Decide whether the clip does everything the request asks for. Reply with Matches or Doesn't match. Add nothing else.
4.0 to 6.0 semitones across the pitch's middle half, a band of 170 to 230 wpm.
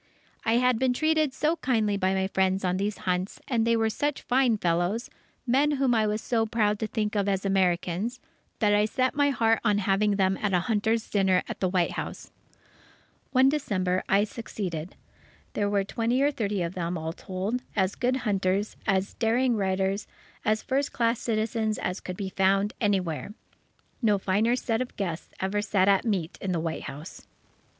Doesn't match